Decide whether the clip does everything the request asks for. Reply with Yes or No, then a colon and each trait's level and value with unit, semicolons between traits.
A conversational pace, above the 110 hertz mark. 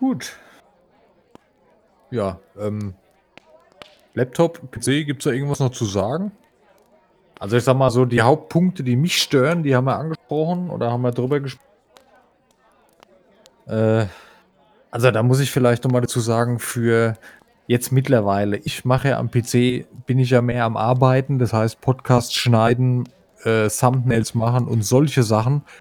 Yes: average, 145 wpm; low, 125 Hz